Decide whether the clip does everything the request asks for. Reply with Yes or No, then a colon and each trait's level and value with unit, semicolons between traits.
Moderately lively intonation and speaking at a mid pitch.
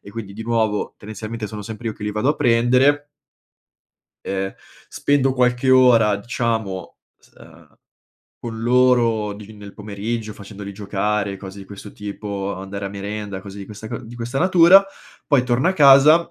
No: average, 3.5 semitones; low, 110 Hz